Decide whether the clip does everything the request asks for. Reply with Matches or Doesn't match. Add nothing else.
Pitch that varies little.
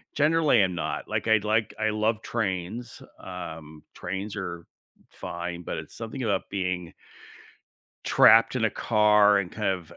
Doesn't match